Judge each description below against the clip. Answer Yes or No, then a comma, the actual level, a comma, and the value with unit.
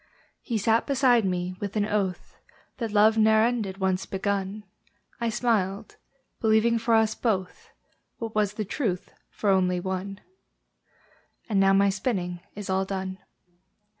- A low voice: No, high, 205 Hz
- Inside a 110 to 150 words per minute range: Yes, average, 140 wpm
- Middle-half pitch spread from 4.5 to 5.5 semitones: No, average, 2.7 semitones